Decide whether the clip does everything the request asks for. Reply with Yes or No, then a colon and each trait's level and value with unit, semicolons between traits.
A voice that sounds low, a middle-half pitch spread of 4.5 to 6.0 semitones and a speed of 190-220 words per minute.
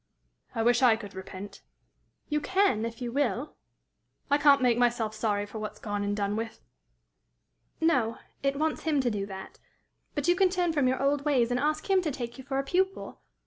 No: very high, 250 Hz; average, 5.2 semitones; average, 200 wpm